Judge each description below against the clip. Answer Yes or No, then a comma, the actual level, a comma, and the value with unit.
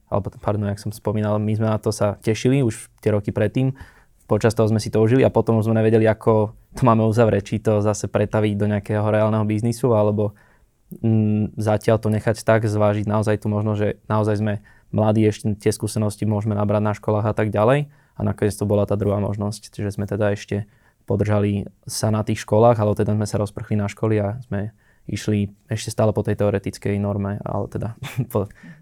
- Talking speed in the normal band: No, fast, 200 wpm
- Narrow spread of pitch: Yes, narrow, 1.2 semitones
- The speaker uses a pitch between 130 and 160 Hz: No, low, 105 Hz